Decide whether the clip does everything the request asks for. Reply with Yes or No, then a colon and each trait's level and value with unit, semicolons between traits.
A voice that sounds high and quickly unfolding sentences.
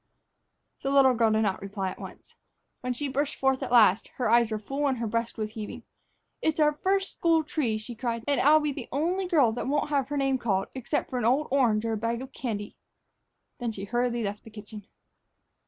Yes: high, 245 Hz; fast, 225 wpm